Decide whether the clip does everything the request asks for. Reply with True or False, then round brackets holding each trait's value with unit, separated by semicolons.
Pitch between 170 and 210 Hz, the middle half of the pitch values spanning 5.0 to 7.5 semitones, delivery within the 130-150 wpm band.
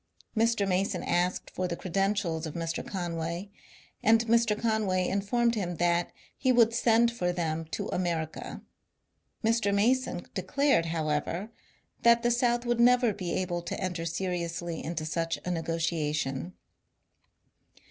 True (185 Hz; 5.3 semitones; 135 wpm)